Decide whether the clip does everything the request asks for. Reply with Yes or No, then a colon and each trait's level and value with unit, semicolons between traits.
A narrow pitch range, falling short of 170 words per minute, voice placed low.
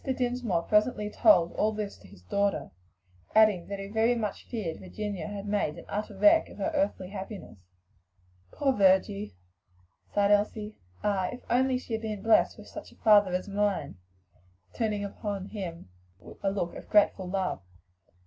No: narrow, 2.3 semitones; average, 160 wpm; high, 205 Hz